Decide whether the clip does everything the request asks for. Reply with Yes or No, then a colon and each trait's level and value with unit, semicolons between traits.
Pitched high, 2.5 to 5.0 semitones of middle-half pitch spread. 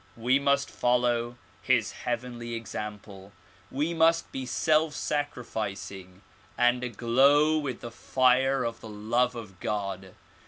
No: low, 120 Hz; average, 3.7 semitones